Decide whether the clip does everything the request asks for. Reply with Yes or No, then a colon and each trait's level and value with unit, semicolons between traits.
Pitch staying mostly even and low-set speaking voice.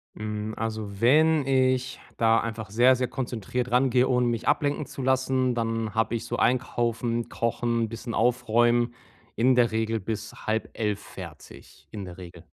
Yes: narrow, 2.2 semitones; low, 120 Hz